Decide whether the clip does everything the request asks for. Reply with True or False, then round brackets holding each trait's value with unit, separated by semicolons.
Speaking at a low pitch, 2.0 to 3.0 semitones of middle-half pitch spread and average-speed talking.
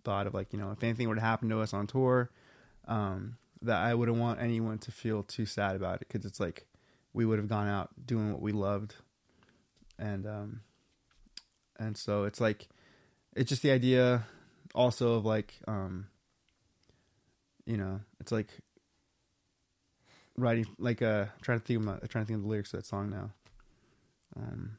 True (110 Hz; 2.5 semitones; 170 wpm)